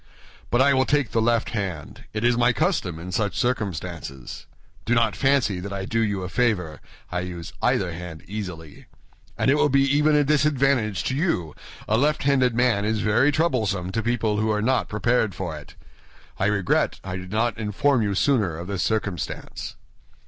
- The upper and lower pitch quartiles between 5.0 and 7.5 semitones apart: Yes, wide, 5.5 semitones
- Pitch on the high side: No, low, 110 Hz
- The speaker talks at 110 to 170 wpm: No, average, 185 wpm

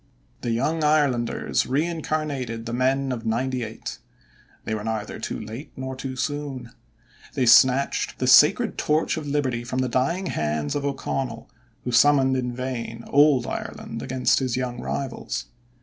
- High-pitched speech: No, low, 130 Hz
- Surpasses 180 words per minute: No, average, 150 wpm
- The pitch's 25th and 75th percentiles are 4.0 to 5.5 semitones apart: No, average, 3.1 semitones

